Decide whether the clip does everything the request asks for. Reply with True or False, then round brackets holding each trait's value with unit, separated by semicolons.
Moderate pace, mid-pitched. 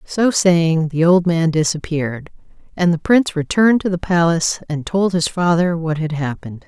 True (180 wpm; 170 Hz)